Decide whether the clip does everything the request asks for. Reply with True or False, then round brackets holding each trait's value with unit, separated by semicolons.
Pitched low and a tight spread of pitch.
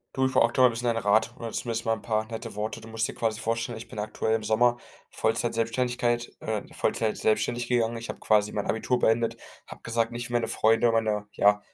True (115 Hz; 1.4 semitones)